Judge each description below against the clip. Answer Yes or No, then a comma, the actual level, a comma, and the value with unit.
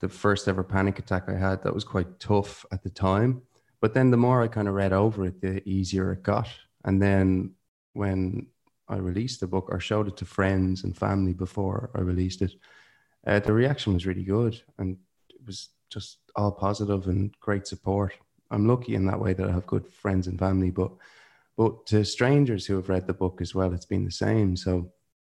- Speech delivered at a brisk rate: Yes, fast, 210 wpm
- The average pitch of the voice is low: Yes, very low, 95 Hz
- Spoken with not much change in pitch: Yes, narrow, 2.1 semitones